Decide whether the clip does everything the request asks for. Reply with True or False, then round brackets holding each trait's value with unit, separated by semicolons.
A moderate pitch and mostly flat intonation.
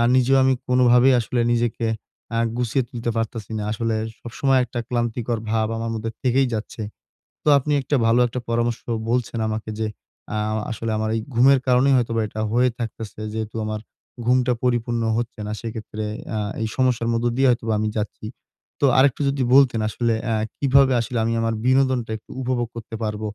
False (120 Hz; 2.1 semitones)